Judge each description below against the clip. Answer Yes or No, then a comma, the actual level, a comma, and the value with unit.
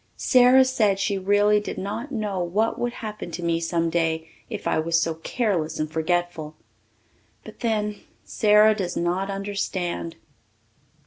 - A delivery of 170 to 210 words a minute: No, average, 145 wpm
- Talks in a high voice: Yes, high, 195 Hz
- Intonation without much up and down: No, average, 4.1 semitones